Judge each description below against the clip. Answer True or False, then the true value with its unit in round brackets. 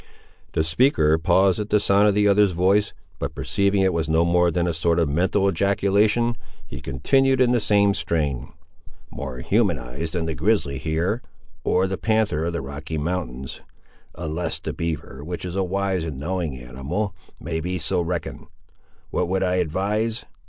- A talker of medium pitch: False (90 Hz)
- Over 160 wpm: True (175 wpm)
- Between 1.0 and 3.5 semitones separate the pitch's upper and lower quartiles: False (4.1 semitones)